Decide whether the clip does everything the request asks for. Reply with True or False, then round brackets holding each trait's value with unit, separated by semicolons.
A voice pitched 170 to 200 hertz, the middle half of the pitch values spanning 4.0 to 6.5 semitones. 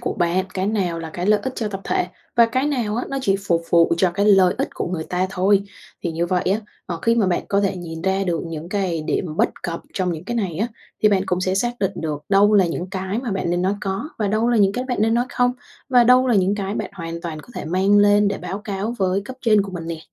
False (195 Hz; 3.3 semitones)